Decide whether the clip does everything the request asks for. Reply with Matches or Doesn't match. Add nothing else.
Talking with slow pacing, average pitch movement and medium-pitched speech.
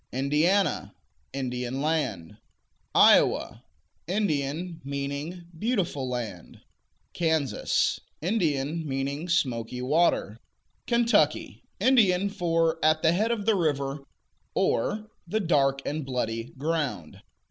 Matches